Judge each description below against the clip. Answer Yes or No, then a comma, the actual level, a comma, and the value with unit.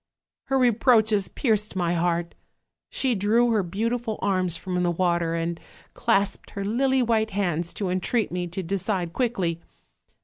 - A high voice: Yes, high, 195 Hz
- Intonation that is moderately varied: Yes, average, 4.4 semitones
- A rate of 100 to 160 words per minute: Yes, average, 150 wpm